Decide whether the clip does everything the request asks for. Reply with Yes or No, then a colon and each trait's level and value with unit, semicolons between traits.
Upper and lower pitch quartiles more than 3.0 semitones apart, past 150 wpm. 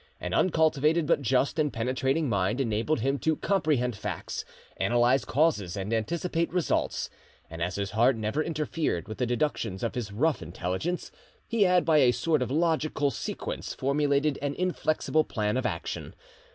Yes: wide, 5.6 semitones; average, 160 wpm